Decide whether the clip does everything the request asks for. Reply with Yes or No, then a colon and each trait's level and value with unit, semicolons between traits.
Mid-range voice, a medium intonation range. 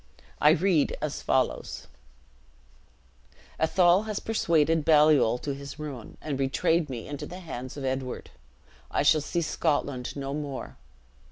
Yes: medium, 150 Hz; average, 3.1 semitones